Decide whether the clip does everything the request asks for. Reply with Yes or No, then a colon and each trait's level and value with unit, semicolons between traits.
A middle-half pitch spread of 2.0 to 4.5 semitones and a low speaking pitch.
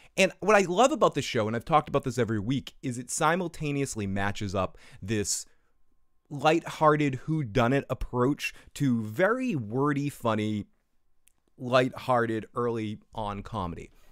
No: average, 5.1 semitones; low, 125 Hz